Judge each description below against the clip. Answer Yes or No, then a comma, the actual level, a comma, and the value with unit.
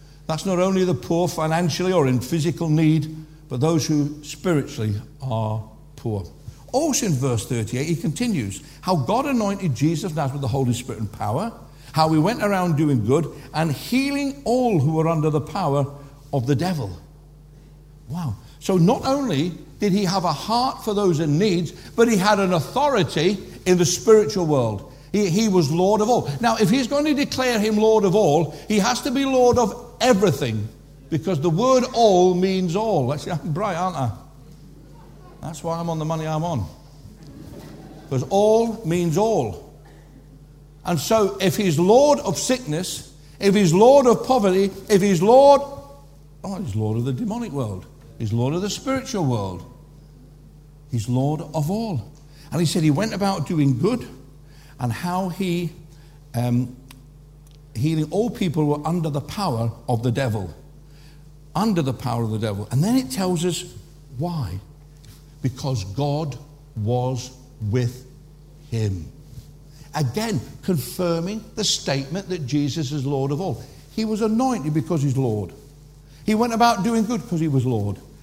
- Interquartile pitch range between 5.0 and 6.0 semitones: Yes, wide, 5.5 semitones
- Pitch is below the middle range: No, medium, 155 Hz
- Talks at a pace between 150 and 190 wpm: Yes, average, 165 wpm